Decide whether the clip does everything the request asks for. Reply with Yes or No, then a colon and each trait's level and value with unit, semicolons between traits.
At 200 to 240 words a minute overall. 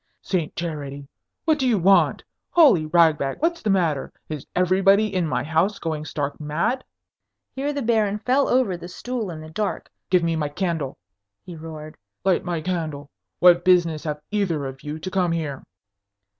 No: average, 170 wpm